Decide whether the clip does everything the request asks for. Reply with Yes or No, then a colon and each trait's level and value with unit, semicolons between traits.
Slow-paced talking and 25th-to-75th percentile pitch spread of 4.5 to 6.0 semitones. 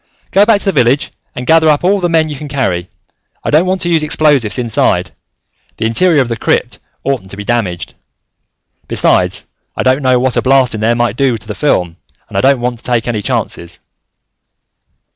No: fast, 205 wpm; average, 5.2 semitones